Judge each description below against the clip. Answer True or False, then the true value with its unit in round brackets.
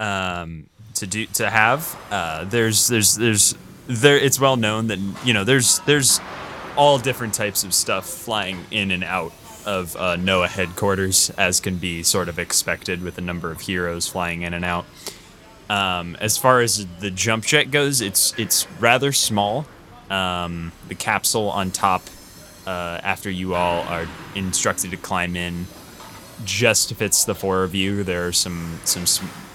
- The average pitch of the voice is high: False (95 Hz)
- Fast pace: False (170 wpm)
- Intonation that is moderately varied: True (3.9 semitones)